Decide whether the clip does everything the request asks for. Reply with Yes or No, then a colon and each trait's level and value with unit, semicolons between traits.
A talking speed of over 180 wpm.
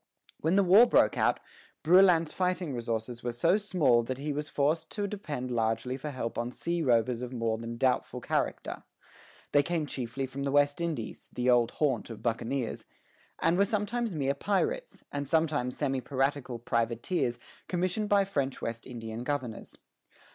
No: average, 165 wpm